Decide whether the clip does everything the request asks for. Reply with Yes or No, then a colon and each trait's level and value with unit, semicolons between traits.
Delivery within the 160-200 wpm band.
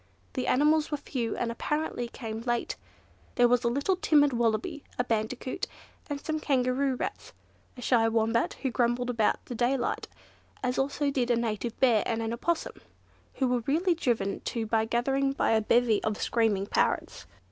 Yes: average, 170 wpm